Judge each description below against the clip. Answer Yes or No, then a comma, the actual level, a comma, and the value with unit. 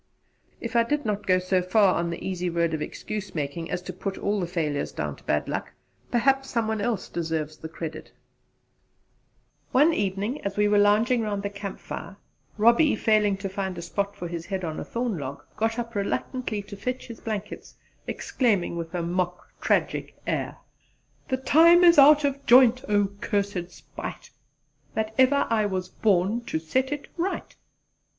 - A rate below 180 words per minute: No, average, 185 wpm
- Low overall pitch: No, high, 205 Hz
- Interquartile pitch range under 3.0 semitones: No, average, 4.7 semitones